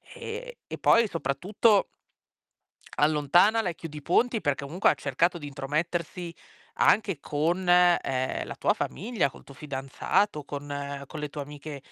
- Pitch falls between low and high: Yes, medium, 155 Hz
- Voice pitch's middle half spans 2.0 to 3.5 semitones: No, average, 4.2 semitones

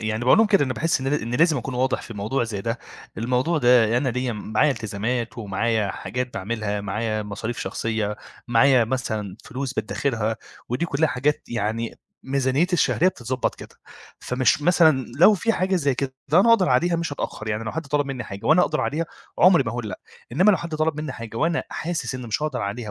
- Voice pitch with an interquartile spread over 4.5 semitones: Yes, average, 5.2 semitones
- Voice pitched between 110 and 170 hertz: Yes, low, 125 Hz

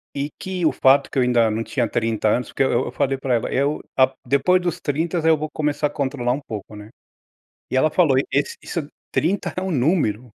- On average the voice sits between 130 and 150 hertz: Yes, medium, 140 Hz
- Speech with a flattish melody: No, average, 4.2 semitones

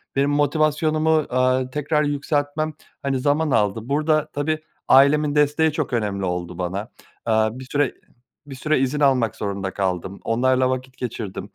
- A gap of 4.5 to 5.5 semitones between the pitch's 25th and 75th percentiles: Yes, average, 4.9 semitones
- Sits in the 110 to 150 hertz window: Yes, low, 135 Hz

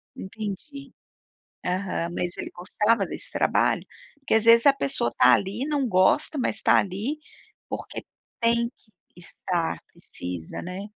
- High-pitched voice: Yes, high, 200 Hz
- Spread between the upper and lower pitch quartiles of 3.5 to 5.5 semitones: Yes, average, 4.7 semitones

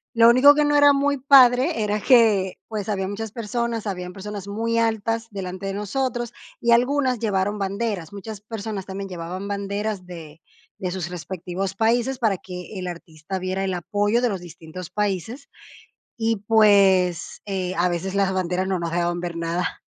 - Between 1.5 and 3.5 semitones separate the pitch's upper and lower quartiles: No, average, 3.9 semitones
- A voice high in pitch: Yes, high, 200 Hz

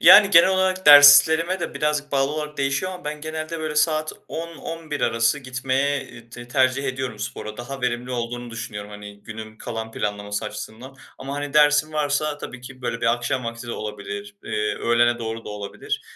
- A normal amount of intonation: Yes, average, 4.5 semitones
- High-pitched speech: No, low, 130 Hz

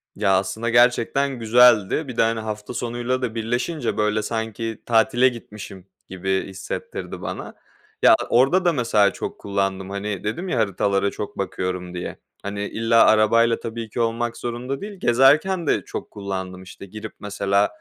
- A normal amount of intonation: Yes, average, 3.4 semitones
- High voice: No, low, 110 Hz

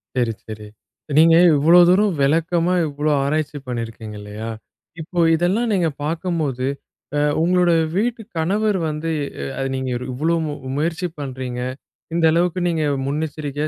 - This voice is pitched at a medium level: Yes, medium, 155 Hz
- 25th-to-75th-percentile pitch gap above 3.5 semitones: Yes, average, 4.1 semitones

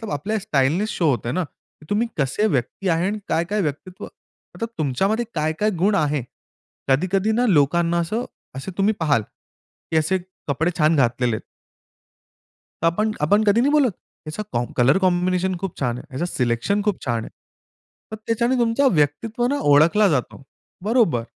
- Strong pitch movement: Yes, wide, 6.5 semitones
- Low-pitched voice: No, medium, 175 Hz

